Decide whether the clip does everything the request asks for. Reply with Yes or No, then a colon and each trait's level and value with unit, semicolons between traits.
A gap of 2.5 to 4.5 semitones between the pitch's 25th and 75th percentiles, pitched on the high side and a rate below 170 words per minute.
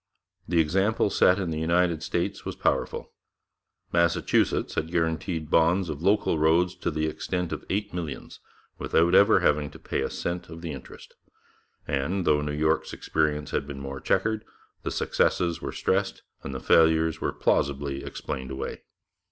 No: average, 3.1 semitones; very low, 80 Hz; average, 160 wpm